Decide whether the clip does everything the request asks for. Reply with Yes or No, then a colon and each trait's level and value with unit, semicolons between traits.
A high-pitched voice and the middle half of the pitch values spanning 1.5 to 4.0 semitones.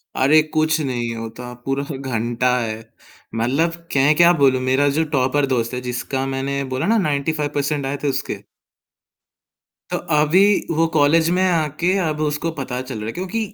No: medium, 140 Hz; average, 3.4 semitones